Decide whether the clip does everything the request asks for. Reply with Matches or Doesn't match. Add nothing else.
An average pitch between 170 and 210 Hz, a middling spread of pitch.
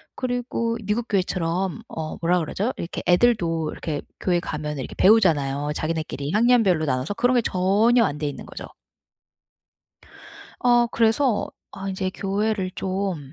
Doesn't match